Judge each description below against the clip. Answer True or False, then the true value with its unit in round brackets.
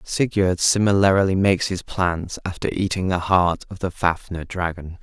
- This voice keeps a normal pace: True (155 wpm)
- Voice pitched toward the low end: True (90 Hz)